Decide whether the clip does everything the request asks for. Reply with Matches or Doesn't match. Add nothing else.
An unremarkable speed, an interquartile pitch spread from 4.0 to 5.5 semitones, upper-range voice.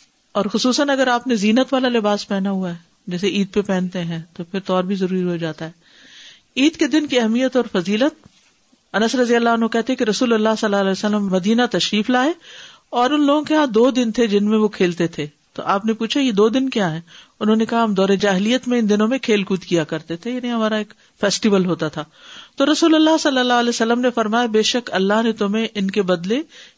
Doesn't match